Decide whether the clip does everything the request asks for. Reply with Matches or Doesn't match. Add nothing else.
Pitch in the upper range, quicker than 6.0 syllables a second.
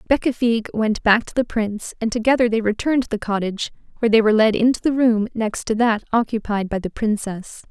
Matches